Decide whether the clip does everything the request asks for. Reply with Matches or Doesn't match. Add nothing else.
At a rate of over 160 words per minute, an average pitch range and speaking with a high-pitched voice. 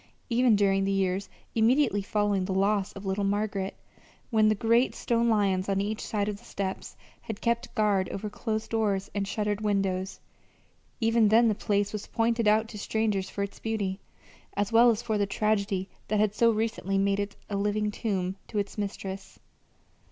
Doesn't match